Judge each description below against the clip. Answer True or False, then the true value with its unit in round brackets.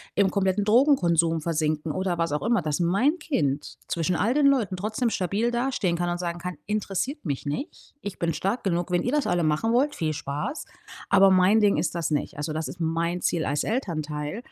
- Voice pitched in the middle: True (180 Hz)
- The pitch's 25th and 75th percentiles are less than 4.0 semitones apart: False (5.1 semitones)